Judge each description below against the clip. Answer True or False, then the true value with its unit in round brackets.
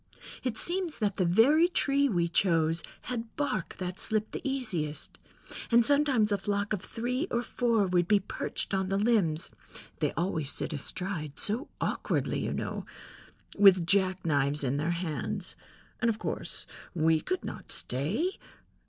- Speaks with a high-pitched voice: True (200 Hz)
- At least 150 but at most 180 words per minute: True (155 wpm)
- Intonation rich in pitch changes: True (5.9 semitones)